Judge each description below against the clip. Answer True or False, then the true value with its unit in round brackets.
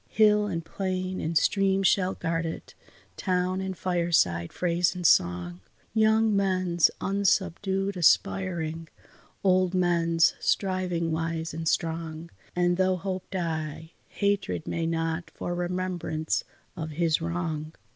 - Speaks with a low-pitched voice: False (175 Hz)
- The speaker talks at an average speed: False (120 wpm)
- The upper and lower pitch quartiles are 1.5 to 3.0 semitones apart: True (2.4 semitones)